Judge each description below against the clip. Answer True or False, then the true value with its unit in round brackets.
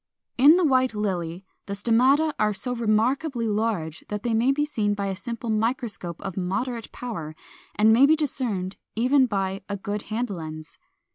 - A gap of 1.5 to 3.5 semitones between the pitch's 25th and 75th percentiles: False (4.3 semitones)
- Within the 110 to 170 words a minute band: False (180 wpm)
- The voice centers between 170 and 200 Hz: False (220 Hz)